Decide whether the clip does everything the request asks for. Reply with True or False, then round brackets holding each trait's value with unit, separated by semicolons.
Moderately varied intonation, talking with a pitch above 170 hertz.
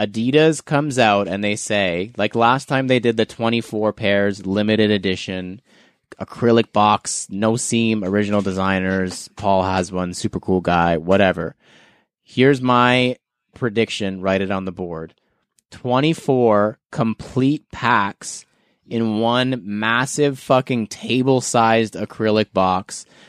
False (4.2 semitones; 110 Hz)